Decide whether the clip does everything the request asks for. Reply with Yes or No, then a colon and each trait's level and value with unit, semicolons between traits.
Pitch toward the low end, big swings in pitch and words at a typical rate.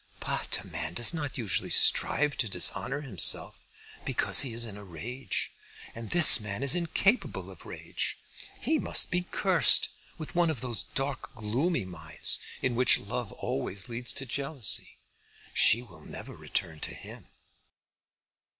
Yes: low, 125 Hz; wide, 6.2 semitones; average, 150 wpm